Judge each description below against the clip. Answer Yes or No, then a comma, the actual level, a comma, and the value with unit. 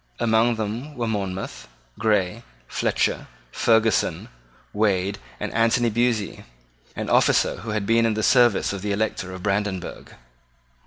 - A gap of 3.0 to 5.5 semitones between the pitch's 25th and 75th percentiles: No, narrow, 2.5 semitones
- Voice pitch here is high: No, low, 110 Hz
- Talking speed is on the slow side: Yes, slow, 130 wpm